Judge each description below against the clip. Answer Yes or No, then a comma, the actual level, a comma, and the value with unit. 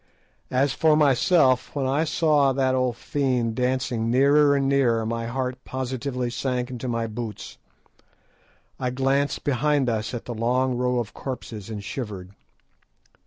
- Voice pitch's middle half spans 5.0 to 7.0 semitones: No, narrow, 2.5 semitones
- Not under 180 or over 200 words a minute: No, average, 145 wpm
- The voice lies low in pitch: Yes, low, 130 Hz